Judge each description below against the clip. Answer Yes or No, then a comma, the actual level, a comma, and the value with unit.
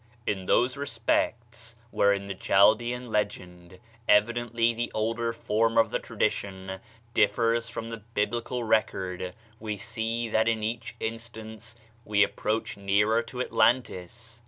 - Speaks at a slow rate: Yes, slow, 125 wpm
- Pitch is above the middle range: No, low, 110 Hz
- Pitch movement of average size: No, narrow, 2.2 semitones